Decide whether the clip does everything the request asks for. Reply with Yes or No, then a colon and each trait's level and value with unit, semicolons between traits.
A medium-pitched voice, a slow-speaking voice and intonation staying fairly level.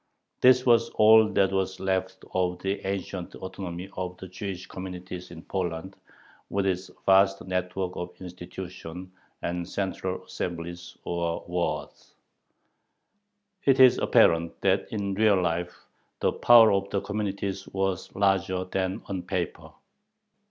No: very low, 95 Hz; slow, 130 wpm; narrow, 1.6 semitones